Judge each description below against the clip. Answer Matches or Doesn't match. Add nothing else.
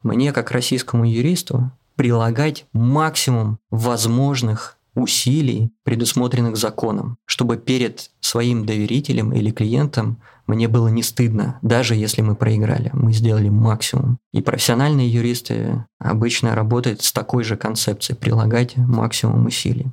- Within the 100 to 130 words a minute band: Matches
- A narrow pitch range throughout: Matches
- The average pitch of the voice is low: Matches